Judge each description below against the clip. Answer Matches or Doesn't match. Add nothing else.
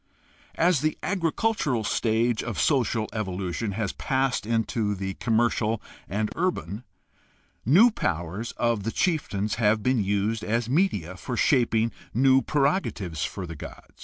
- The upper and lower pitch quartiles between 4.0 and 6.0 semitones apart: Matches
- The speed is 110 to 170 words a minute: Matches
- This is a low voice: Matches